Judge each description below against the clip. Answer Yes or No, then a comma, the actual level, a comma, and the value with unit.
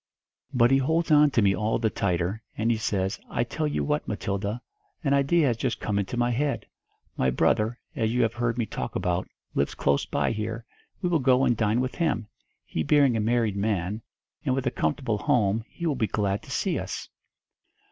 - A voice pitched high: No, low, 115 Hz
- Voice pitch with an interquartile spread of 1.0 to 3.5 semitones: No, average, 4.3 semitones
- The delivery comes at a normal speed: No, fast, 210 wpm